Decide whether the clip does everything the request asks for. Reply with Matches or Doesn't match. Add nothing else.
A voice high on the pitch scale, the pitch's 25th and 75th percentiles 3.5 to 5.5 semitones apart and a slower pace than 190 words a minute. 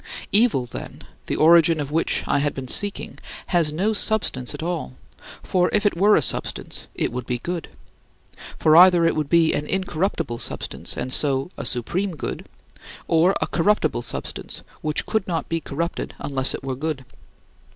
Doesn't match